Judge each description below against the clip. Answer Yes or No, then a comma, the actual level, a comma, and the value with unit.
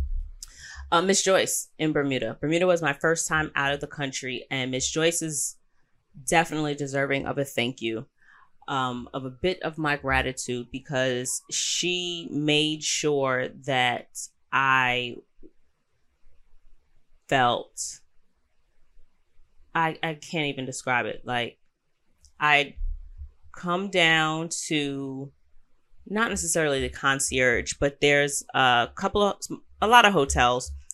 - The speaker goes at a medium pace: No, slow, 120 wpm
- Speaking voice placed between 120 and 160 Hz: Yes, medium, 140 Hz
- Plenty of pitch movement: No, average, 4.5 semitones